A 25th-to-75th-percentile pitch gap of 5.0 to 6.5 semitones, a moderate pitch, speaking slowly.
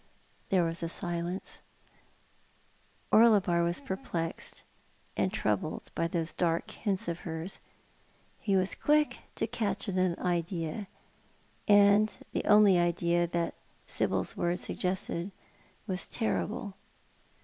No: average, 2.9 semitones; medium, 180 Hz; slow, 115 wpm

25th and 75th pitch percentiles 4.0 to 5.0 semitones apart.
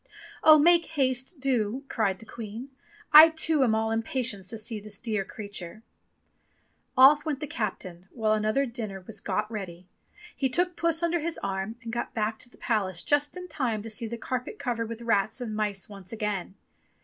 Yes: average, 4.4 semitones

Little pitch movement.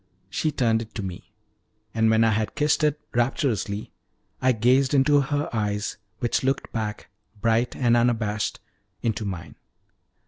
No: average, 3.6 semitones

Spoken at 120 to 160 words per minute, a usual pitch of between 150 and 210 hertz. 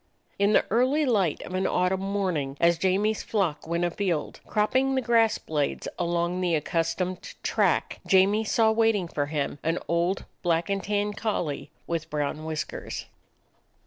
Yes: average, 150 wpm; medium, 185 Hz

